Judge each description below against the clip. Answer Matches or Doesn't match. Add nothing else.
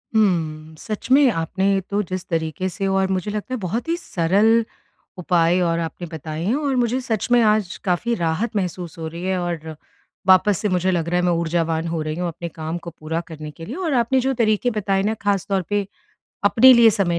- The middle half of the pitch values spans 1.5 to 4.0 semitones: Doesn't match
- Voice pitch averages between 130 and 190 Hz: Matches